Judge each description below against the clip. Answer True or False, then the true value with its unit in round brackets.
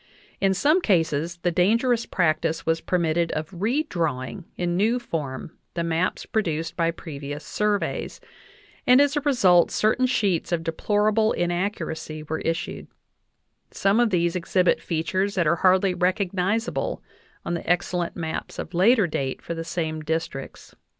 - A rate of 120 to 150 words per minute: True (145 wpm)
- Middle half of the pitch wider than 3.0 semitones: True (3.9 semitones)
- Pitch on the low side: False (175 Hz)